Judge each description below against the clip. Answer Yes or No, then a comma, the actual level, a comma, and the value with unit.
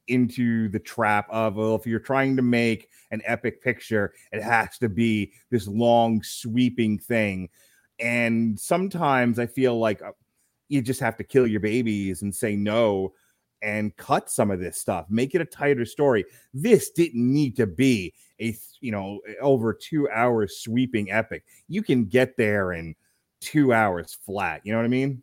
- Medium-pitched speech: No, low, 115 Hz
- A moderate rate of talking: Yes, average, 175 wpm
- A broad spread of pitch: No, average, 2.9 semitones